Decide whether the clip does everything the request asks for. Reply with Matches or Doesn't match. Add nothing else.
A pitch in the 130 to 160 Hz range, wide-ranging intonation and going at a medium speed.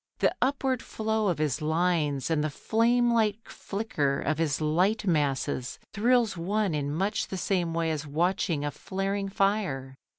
Doesn't match